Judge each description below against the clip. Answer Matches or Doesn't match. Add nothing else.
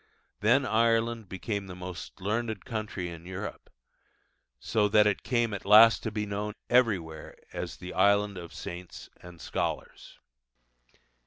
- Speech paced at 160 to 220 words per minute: Doesn't match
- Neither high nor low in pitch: Doesn't match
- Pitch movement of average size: Matches